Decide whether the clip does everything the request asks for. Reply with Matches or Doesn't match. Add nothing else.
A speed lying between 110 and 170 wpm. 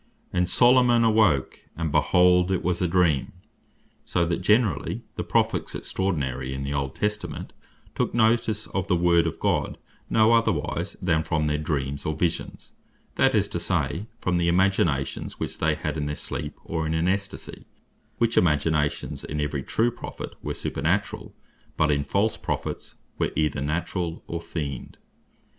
Matches